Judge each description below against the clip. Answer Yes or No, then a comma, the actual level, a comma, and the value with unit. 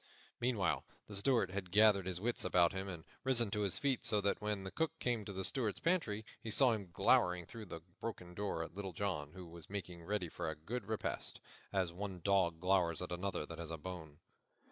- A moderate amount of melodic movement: Yes, average, 3.3 semitones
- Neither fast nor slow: No, fast, 215 wpm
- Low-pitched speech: Yes, very low, 95 Hz